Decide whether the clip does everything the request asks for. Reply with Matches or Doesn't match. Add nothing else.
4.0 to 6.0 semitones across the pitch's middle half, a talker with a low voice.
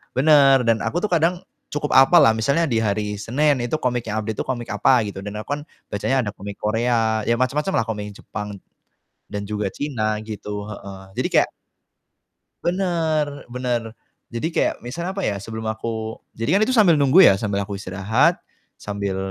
Matches